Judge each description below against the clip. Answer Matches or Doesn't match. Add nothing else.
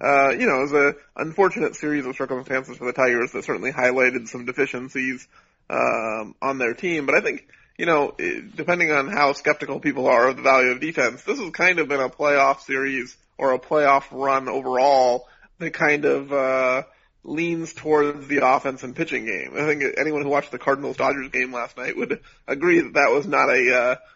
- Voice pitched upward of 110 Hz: Matches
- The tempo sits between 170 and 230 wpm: Matches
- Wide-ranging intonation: Doesn't match